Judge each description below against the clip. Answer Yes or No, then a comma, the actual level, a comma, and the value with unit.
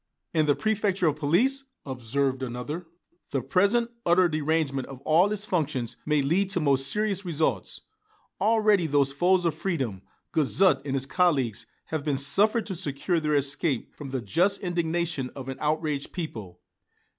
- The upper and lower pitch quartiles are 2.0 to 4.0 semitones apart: No, average, 5.0 semitones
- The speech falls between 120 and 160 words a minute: Yes, average, 155 wpm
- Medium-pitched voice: Yes, medium, 155 Hz